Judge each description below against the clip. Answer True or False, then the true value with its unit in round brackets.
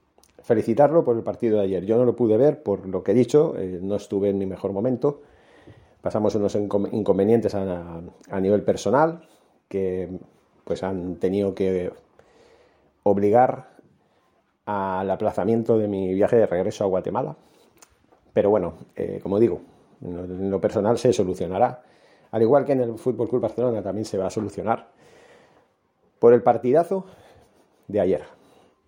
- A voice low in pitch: True (105 Hz)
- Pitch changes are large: False (4.4 semitones)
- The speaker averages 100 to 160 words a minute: True (150 wpm)